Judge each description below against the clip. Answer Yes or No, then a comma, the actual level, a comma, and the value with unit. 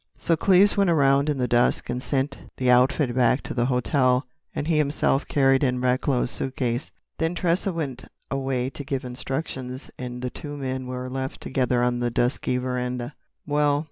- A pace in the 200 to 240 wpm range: No, average, 175 wpm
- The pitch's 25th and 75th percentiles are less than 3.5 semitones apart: Yes, narrow, 2.4 semitones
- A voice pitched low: Yes, low, 130 Hz